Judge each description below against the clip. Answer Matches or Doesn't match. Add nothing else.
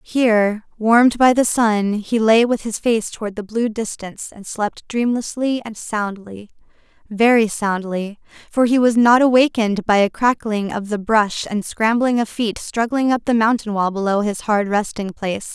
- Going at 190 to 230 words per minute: Doesn't match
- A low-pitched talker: Doesn't match